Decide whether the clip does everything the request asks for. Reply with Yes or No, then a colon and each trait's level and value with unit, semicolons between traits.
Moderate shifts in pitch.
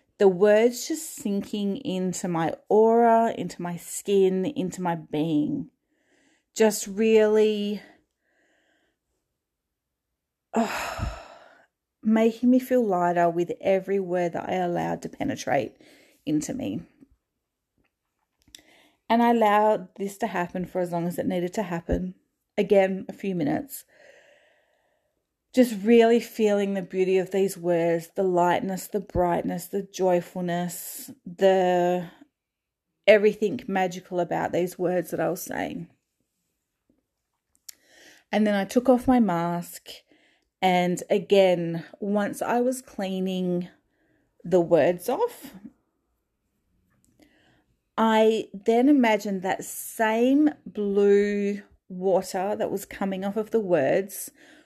Yes: average, 4.4 semitones